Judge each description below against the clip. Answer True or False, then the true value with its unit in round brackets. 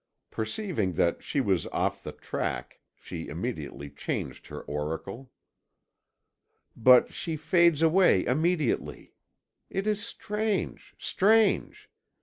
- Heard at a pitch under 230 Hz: True (140 Hz)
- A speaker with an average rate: False (105 wpm)